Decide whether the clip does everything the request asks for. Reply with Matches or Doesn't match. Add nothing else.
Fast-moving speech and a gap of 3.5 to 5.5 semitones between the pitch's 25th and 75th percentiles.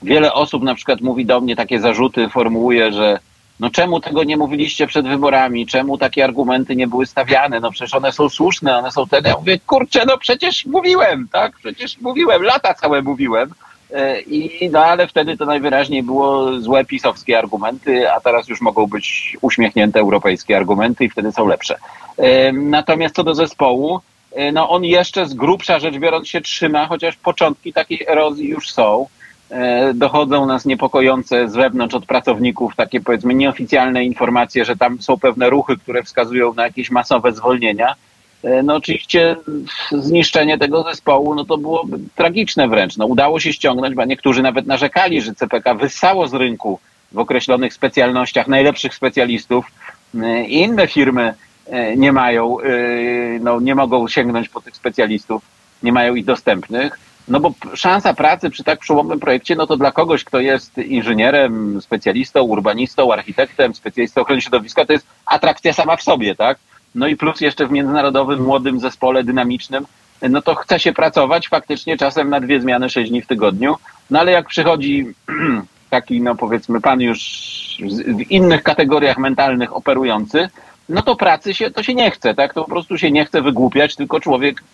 Matches